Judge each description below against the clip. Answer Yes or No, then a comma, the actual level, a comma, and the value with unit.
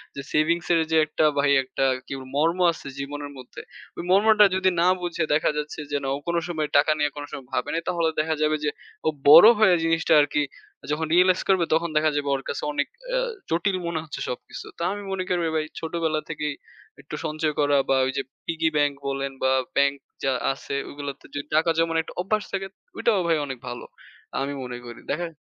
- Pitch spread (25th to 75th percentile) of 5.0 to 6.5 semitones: No, average, 2.9 semitones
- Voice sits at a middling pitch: Yes, medium, 155 Hz